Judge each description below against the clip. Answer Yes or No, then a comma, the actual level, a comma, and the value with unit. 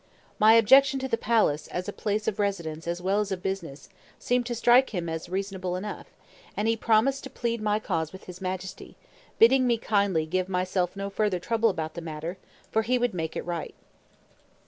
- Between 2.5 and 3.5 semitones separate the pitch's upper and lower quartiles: No, average, 4.2 semitones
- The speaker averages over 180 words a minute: Yes, average, 200 wpm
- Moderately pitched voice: No, high, 200 Hz